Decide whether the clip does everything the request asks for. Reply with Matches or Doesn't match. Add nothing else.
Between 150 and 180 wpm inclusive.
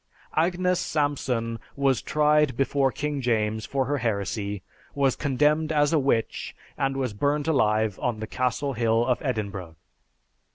Doesn't match